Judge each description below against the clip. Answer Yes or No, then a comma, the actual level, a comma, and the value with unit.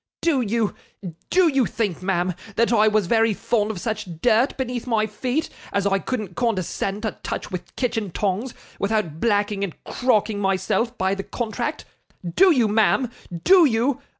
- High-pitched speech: Yes, high, 220 Hz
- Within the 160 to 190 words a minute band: Yes, average, 165 wpm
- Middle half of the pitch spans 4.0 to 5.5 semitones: No, average, 3.6 semitones